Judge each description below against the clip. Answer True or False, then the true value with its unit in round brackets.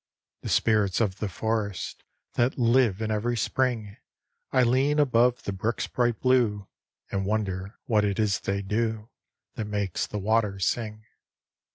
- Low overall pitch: True (110 Hz)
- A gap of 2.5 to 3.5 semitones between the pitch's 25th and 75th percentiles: True (2.9 semitones)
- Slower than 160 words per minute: True (150 wpm)